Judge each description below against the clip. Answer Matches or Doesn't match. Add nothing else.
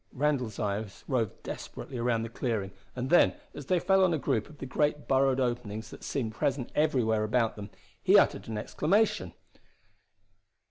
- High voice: Doesn't match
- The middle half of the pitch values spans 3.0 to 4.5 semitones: Doesn't match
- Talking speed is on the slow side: Doesn't match